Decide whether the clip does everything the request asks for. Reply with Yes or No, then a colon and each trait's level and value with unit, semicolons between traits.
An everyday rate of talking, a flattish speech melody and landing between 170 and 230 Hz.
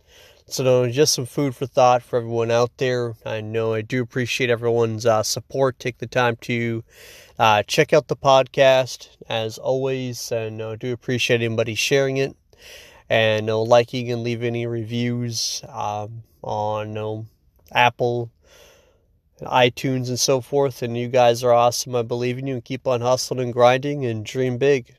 No: average, 175 wpm; narrow, 2.3 semitones; low, 120 Hz